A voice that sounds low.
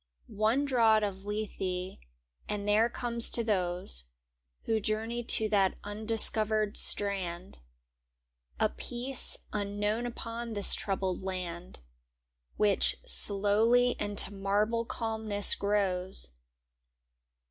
No: high, 210 Hz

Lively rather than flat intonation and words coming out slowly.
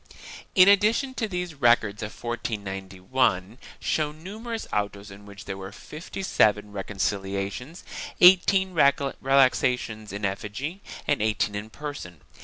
Yes: wide, 8.0 semitones; slow, 125 wpm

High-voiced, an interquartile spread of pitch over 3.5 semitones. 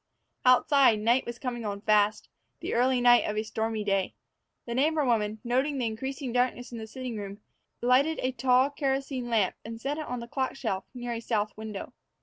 No: high, 240 Hz; average, 3.1 semitones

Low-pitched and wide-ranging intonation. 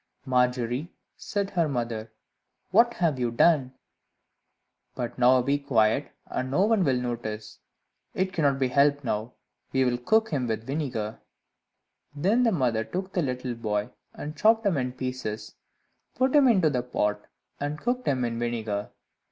Yes: low, 130 Hz; wide, 6.0 semitones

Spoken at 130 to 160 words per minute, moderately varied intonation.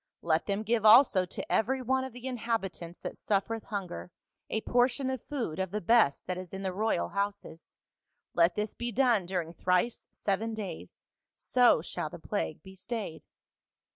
No: average, 170 wpm; average, 4.5 semitones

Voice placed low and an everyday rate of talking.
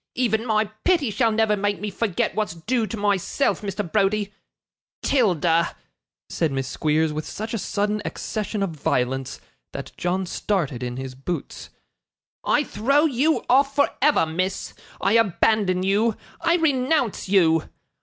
No: high, 205 Hz; average, 145 wpm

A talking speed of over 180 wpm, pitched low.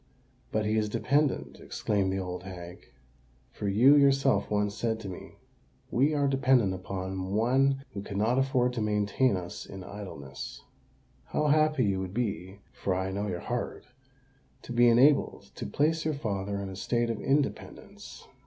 No: average, 155 wpm; low, 110 Hz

